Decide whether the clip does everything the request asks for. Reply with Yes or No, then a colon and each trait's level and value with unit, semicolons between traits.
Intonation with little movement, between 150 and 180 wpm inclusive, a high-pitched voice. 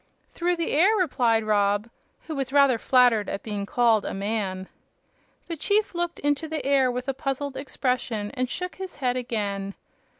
No: average, 5.2 semitones; average, 170 wpm; very high, 255 Hz